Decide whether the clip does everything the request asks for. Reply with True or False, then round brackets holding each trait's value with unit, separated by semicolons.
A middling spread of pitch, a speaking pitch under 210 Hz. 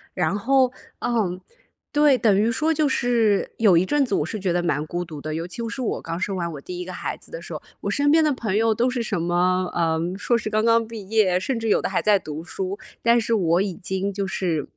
True (4.7 semitones; 200 Hz)